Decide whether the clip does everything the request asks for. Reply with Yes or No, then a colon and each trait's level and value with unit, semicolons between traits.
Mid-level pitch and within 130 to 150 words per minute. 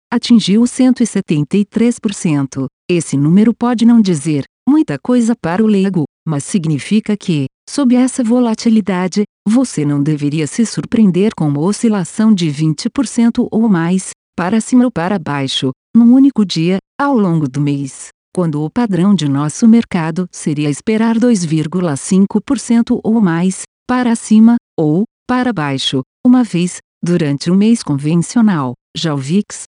No: high, 200 Hz; average, 135 wpm